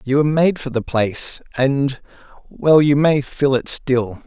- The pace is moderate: Yes, average, 170 wpm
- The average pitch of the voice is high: No, low, 135 Hz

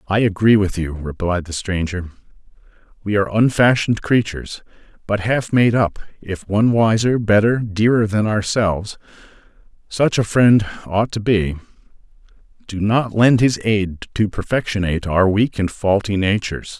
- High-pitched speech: No, low, 105 Hz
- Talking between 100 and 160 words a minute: Yes, slow, 135 wpm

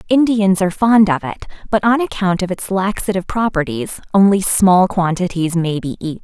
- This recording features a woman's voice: Yes, female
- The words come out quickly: No, average, 175 wpm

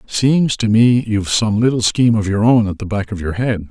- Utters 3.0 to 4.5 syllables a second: No, 5.4 syllables/s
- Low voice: Yes, low, 110 Hz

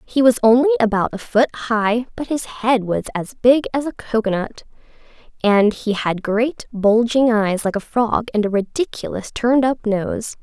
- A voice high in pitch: Yes, high, 230 Hz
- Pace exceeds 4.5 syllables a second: No, 4.4 syllables/s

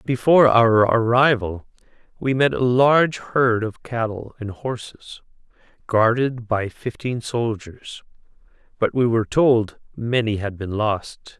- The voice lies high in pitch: No, low, 115 Hz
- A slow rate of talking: Yes, slow, 125 wpm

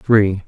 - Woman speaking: No, male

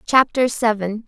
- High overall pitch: Yes, high, 230 Hz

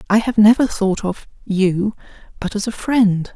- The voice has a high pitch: Yes, high, 210 Hz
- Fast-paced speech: No, average, 160 wpm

